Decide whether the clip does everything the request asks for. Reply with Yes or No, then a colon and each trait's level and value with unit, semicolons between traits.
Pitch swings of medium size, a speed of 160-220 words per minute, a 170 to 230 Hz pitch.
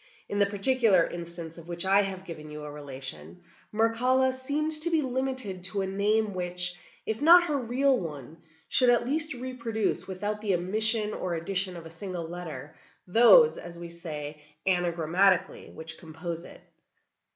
No: wide, 6.0 semitones; average, 165 wpm; high, 190 Hz